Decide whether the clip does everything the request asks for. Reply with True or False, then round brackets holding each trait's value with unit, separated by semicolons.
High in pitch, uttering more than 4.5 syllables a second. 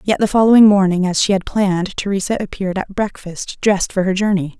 True (195 Hz; 6.1 syllables/s)